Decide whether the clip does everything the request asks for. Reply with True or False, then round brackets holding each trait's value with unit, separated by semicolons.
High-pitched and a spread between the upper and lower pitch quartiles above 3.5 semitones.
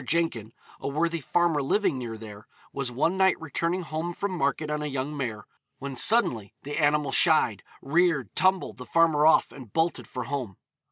False (150 Hz; 4.8 semitones)